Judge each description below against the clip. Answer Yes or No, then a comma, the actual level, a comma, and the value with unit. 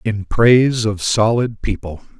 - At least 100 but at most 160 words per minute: Yes, slow, 135 wpm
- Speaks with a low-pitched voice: Yes, low, 110 Hz